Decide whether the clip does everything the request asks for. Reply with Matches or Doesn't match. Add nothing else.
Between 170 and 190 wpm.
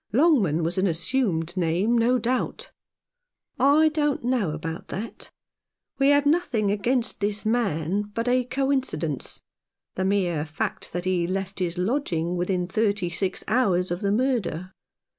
Doesn't match